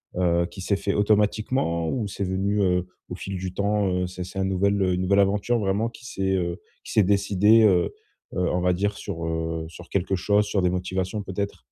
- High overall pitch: No, very low, 95 Hz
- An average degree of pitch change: No, narrow, 2.1 semitones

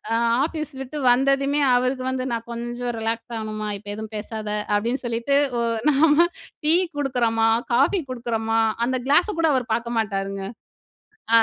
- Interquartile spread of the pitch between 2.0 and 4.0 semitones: Yes, average, 3.5 semitones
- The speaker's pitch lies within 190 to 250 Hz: Yes, high, 240 Hz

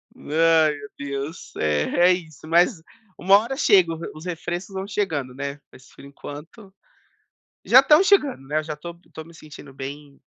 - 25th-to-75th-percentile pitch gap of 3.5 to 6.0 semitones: Yes, average, 4.2 semitones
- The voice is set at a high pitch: No, medium, 160 Hz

